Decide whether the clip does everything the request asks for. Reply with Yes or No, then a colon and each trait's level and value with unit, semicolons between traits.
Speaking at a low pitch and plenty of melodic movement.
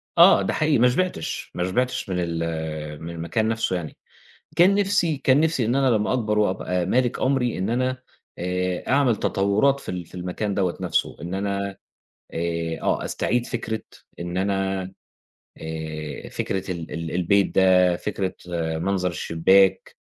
Yes: very low, 95 Hz; wide, 5.8 semitones